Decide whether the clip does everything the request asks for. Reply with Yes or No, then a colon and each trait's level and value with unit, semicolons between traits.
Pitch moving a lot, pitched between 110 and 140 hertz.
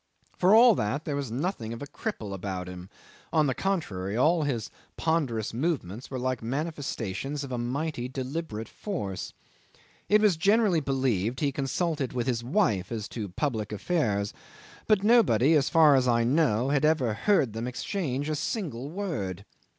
Yes: wide, 6.1 semitones; low, 135 Hz